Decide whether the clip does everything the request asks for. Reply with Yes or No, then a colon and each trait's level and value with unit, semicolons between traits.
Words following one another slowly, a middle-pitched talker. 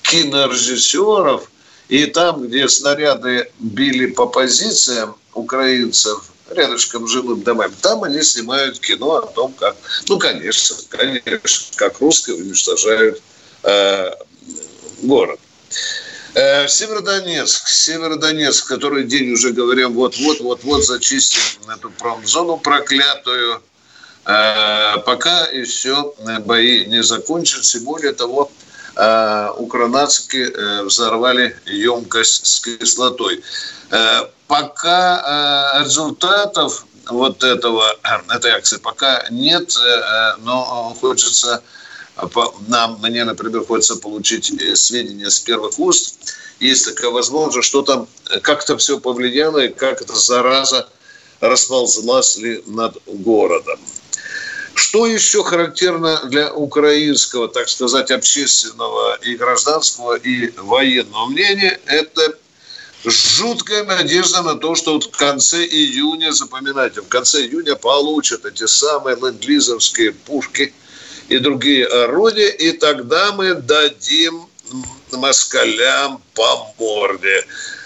Yes: slow, 100 wpm; medium, 145 Hz